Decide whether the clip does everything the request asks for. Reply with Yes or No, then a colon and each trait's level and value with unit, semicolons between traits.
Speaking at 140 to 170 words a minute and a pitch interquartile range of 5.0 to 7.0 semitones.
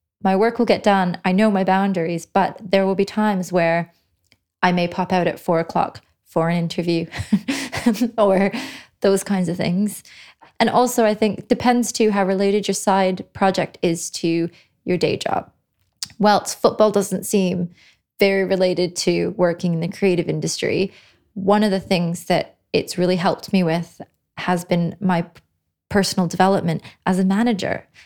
No: average, 165 wpm; average, 2.8 semitones